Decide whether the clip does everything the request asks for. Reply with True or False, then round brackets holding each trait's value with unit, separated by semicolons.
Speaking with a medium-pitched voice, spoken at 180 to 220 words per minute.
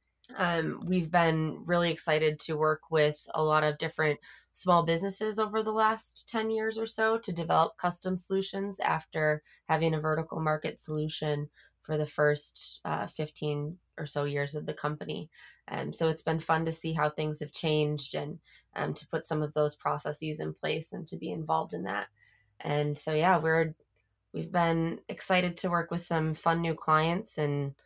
True (160 Hz; 185 wpm)